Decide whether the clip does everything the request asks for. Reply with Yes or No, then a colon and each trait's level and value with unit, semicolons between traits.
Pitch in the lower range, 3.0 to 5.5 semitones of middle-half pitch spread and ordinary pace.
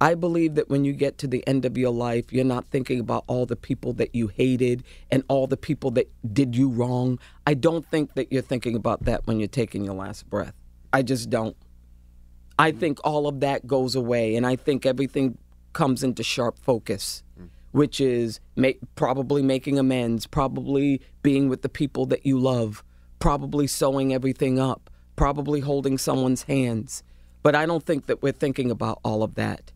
Yes: low, 130 Hz; average, 3.4 semitones; average, 190 wpm